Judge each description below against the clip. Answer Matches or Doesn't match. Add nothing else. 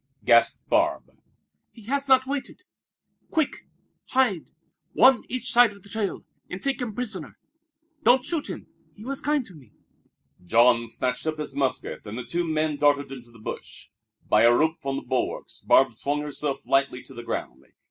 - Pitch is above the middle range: Doesn't match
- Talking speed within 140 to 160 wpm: Doesn't match